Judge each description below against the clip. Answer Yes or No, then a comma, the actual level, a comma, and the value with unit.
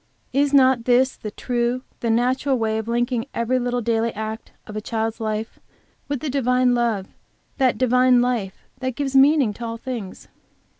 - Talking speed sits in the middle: Yes, average, 170 wpm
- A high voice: Yes, high, 245 Hz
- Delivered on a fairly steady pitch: Yes, narrow, 2.3 semitones